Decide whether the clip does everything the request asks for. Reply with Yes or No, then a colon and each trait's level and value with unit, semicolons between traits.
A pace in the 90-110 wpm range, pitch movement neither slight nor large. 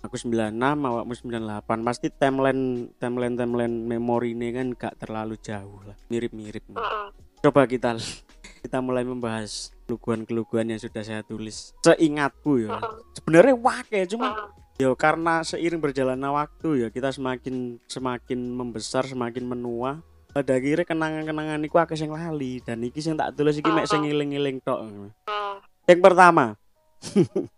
No: average, 135 wpm; average, 4.6 semitones